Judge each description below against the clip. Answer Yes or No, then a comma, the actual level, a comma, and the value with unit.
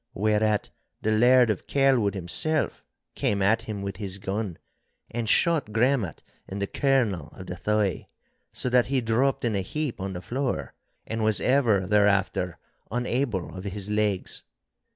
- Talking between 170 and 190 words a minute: No, average, 155 wpm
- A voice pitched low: Yes, low, 105 Hz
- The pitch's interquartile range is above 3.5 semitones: Yes, average, 3.9 semitones